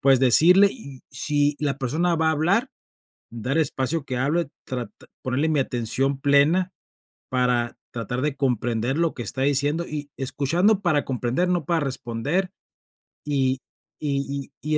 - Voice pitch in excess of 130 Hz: Yes, medium, 140 Hz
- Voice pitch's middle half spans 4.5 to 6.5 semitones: No, average, 3.7 semitones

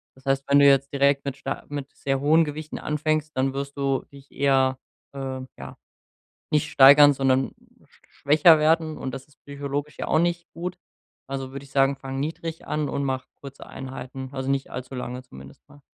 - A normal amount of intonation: No, narrow, 1.6 semitones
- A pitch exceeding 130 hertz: Yes, medium, 140 Hz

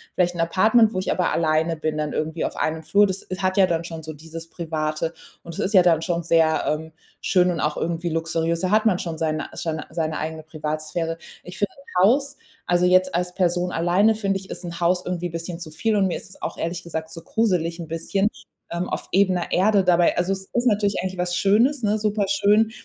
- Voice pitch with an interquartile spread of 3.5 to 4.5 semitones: No, average, 2.9 semitones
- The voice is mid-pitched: Yes, medium, 175 Hz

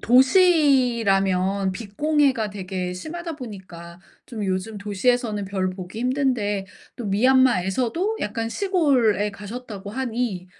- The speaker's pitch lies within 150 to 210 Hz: No, high, 220 Hz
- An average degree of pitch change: Yes, average, 5.0 semitones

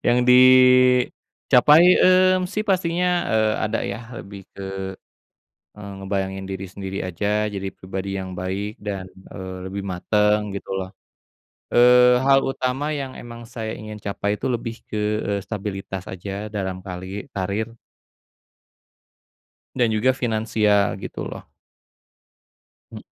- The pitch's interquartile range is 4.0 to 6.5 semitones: Yes, average, 4.3 semitones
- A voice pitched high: No, low, 105 Hz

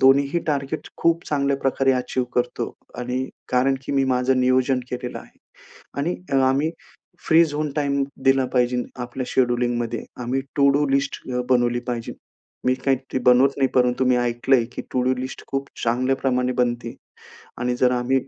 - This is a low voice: Yes, low, 130 Hz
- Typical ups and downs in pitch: No, narrow, 1.8 semitones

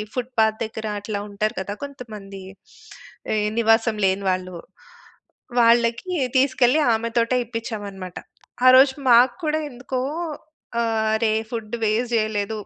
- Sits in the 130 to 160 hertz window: No, high, 225 Hz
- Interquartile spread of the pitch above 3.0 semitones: No, narrow, 2.5 semitones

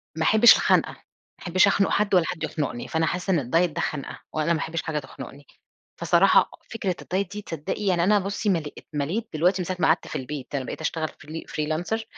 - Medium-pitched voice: Yes, medium, 165 Hz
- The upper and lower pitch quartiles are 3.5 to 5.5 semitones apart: Yes, average, 4.1 semitones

